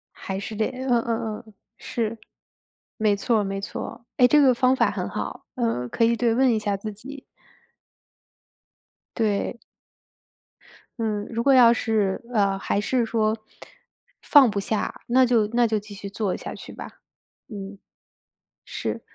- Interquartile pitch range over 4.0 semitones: No, average, 2.8 semitones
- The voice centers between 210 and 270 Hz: Yes, high, 225 Hz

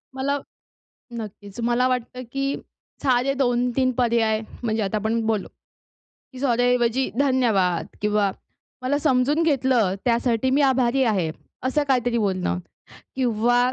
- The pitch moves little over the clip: No, average, 3.0 semitones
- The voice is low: No, high, 245 Hz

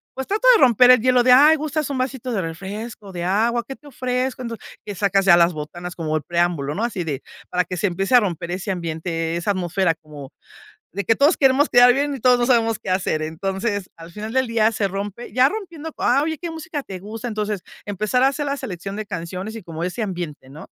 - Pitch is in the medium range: No, high, 205 Hz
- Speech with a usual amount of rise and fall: No, wide, 6.3 semitones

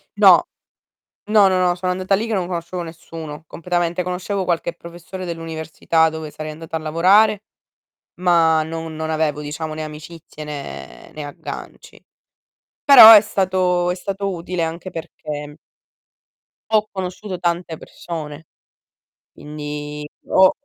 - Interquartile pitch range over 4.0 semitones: No, average, 2.8 semitones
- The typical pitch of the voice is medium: Yes, medium, 170 Hz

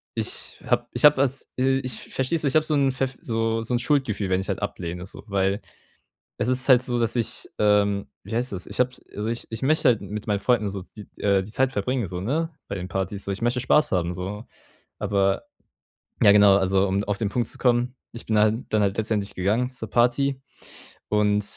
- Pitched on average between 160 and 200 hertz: No, low, 110 Hz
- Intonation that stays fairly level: No, average, 4.1 semitones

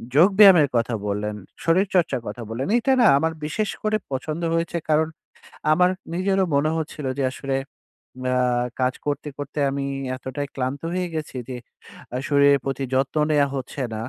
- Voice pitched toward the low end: No, medium, 145 Hz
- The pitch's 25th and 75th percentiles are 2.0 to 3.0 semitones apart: No, average, 4.2 semitones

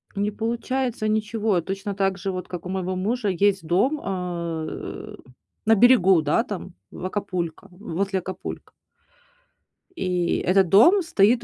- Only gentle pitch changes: No, average, 3.1 semitones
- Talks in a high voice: Yes, high, 195 Hz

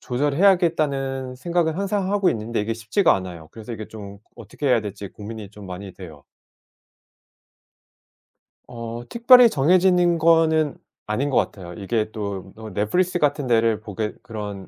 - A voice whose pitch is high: No, low, 115 Hz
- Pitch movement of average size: No, wide, 7.7 semitones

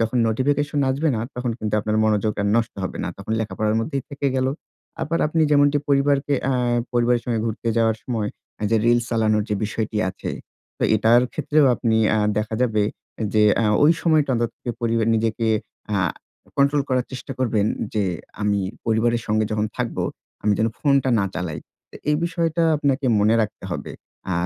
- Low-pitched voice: Yes, low, 115 Hz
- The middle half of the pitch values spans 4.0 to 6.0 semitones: Yes, average, 4.3 semitones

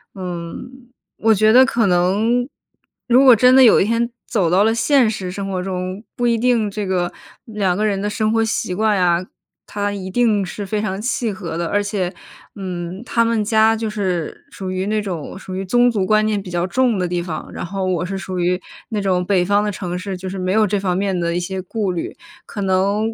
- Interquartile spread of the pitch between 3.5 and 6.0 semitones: No, average, 3.1 semitones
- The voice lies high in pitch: Yes, high, 200 Hz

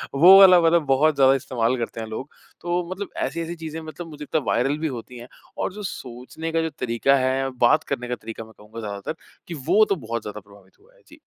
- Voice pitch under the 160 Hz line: Yes, low, 135 Hz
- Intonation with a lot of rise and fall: Yes, wide, 5.7 semitones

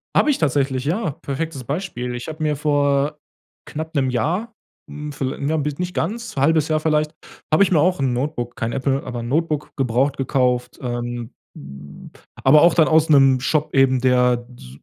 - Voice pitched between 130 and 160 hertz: Yes, medium, 140 Hz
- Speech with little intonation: No, average, 3.7 semitones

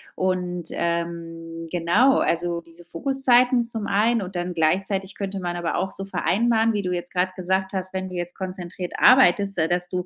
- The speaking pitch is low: No, medium, 185 Hz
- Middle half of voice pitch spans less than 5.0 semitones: Yes, narrow, 2.4 semitones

